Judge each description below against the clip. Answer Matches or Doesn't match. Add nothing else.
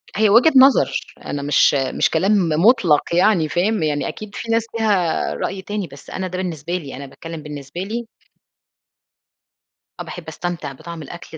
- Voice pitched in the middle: Matches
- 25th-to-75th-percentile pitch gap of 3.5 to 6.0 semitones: Matches